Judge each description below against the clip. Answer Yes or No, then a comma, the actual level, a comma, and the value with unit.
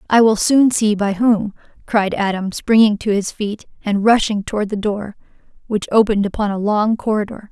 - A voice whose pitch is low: No, high, 210 Hz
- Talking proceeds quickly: No, average, 185 wpm